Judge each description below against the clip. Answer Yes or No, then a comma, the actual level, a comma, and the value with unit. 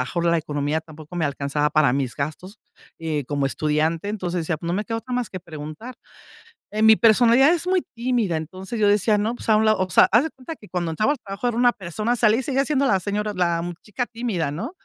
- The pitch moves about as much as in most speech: No, wide, 6.5 semitones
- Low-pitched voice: No, high, 195 Hz